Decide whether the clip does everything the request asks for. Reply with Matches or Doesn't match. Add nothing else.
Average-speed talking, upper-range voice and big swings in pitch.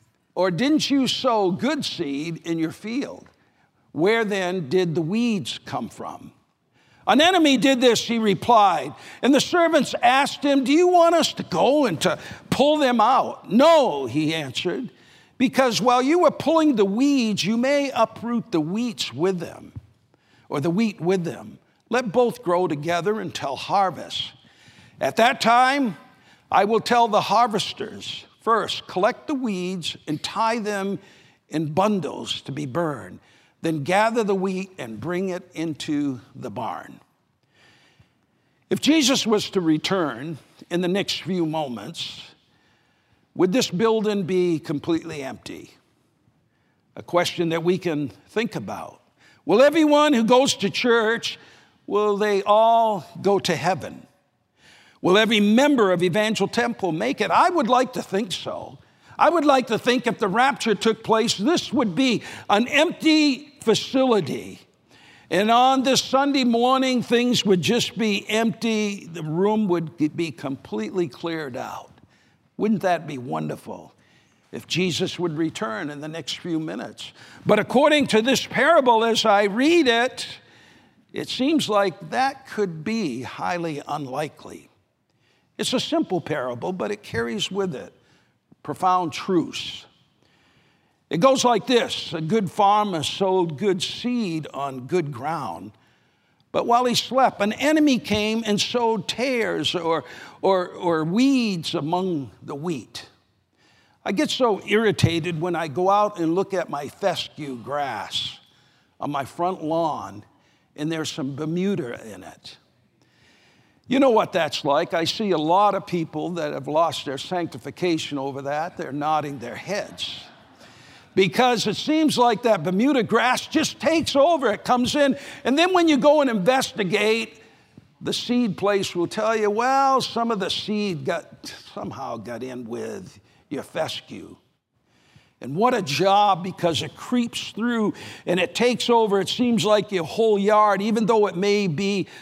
Matches